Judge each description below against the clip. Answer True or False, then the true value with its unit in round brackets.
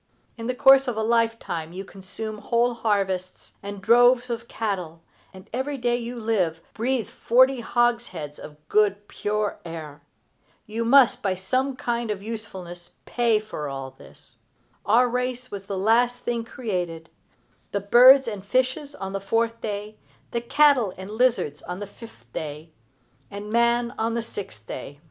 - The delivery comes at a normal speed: True (160 wpm)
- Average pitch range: True (4.1 semitones)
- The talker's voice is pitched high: True (220 Hz)